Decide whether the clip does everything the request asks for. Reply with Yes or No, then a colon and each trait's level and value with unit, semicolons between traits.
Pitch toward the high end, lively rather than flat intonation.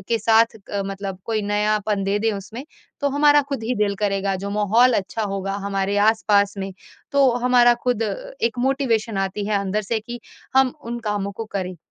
No: high, 210 Hz; average, 3.1 semitones